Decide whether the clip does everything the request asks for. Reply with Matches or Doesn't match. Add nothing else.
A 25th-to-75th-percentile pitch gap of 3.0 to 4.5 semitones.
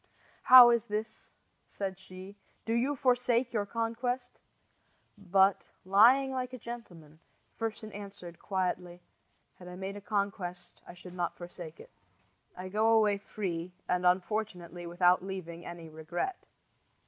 Matches